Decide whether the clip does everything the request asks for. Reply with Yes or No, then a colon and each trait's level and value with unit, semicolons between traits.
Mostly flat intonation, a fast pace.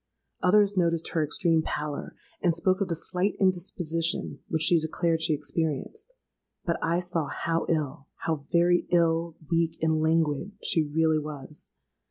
No: narrow, 1.9 semitones; average, 145 wpm